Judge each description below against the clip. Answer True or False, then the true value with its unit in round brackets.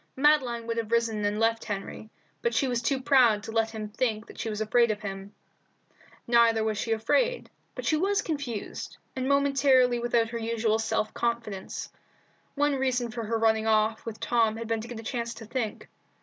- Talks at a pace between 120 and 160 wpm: False (195 wpm)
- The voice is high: True (230 Hz)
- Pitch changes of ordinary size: False (2.2 semitones)